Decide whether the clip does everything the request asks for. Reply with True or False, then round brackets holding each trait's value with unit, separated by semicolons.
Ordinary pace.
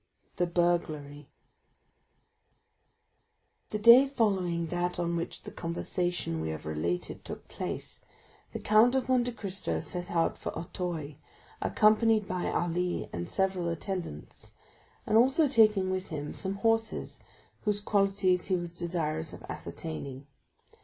False (125 wpm)